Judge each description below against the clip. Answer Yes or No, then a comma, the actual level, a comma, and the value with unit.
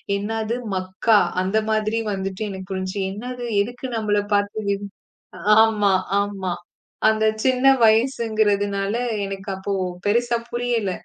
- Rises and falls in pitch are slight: Yes, narrow, 2.3 semitones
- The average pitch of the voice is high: Yes, high, 210 Hz